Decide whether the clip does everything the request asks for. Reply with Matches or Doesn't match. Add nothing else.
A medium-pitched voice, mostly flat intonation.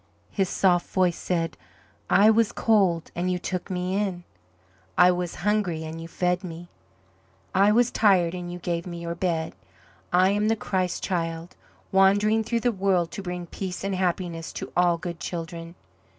Matches